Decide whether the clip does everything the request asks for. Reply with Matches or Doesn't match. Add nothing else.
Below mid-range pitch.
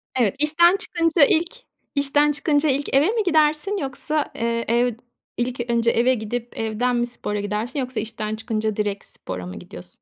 Doesn't match